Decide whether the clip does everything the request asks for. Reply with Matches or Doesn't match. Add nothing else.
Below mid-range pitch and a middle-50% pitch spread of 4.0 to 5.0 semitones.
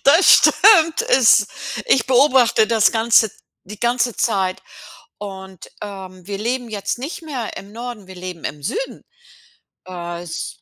Doesn't match